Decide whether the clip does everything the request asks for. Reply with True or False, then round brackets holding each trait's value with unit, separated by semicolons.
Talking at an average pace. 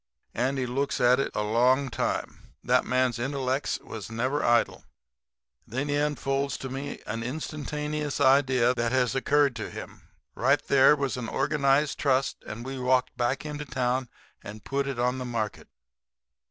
True (165 wpm)